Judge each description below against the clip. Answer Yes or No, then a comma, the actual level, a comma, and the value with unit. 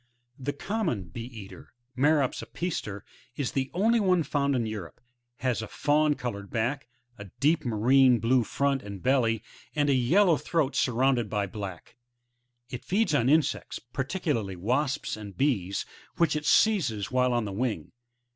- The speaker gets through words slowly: No, average, 160 wpm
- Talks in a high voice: No, low, 130 Hz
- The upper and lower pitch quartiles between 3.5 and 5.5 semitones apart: Yes, average, 5.0 semitones